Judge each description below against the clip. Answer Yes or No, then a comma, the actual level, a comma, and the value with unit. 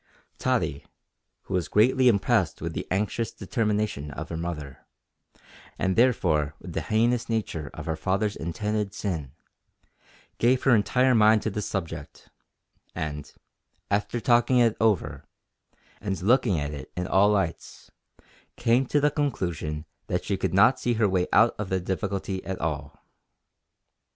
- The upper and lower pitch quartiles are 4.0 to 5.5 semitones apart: Yes, average, 5.2 semitones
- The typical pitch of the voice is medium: No, low, 100 Hz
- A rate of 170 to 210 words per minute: No, average, 145 wpm